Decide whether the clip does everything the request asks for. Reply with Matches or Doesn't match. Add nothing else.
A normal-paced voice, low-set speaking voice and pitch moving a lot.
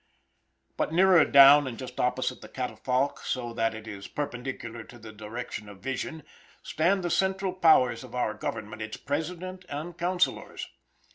Matches